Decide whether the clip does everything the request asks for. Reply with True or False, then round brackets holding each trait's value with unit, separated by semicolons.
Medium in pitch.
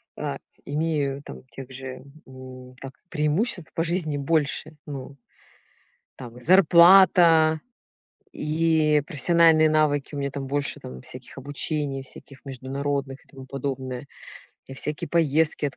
True (145 Hz)